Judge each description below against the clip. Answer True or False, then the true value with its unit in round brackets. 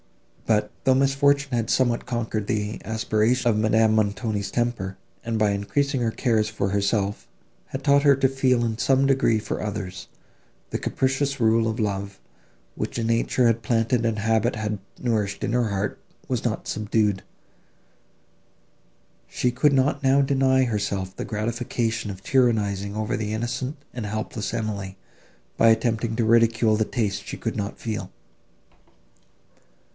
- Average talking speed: True (150 wpm)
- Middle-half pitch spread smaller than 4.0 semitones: True (2.9 semitones)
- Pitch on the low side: True (115 Hz)